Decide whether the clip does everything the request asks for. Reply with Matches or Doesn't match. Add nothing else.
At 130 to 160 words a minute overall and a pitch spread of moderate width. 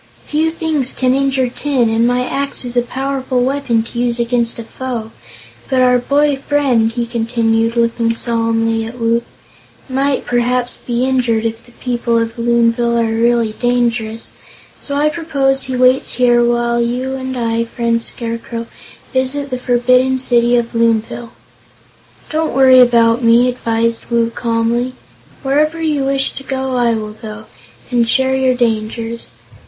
Doesn't match